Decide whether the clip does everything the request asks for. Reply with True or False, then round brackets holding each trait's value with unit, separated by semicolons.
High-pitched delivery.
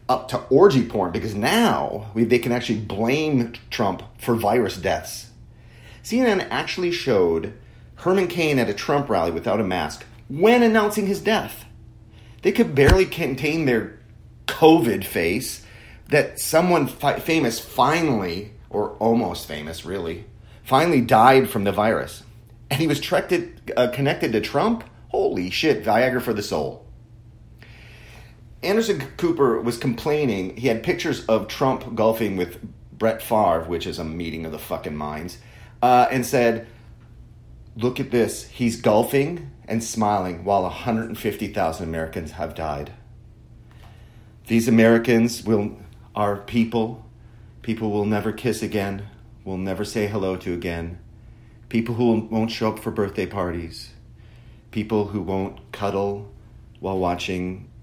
False (115 Hz)